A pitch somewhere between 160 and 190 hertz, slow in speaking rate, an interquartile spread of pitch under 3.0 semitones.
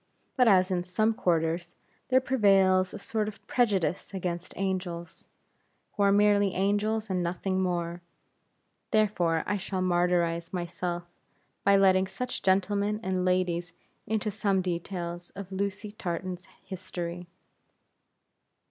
Yes: medium, 185 Hz; slow, 120 wpm; narrow, 2.5 semitones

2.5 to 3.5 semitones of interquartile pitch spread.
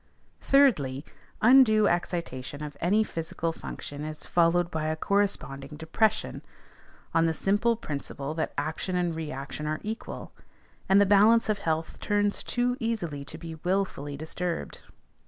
No: average, 5.0 semitones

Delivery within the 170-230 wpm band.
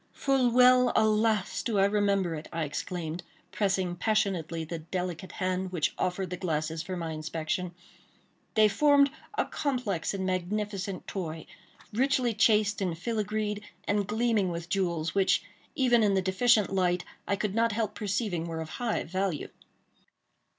No: average, 145 wpm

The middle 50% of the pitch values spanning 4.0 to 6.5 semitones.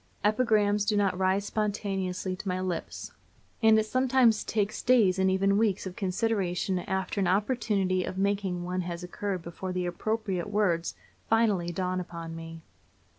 No: narrow, 2.6 semitones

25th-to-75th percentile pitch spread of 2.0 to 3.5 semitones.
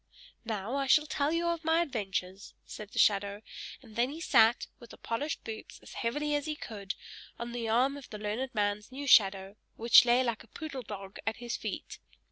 No: average, 4.9 semitones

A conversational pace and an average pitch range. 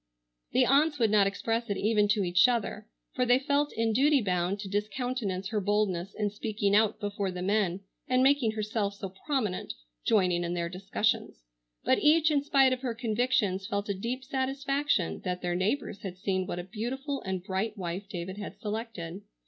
Yes: average, 180 wpm; average, 4.9 semitones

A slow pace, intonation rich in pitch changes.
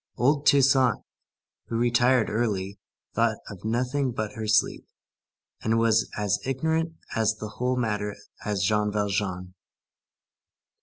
No: slow, 120 wpm; average, 3.4 semitones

